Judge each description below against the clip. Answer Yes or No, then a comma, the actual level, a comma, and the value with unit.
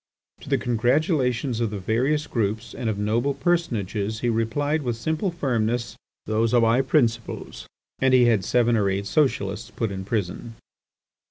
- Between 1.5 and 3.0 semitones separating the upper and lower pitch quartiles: No, average, 3.4 semitones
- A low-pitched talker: Yes, low, 115 Hz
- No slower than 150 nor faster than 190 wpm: Yes, average, 160 wpm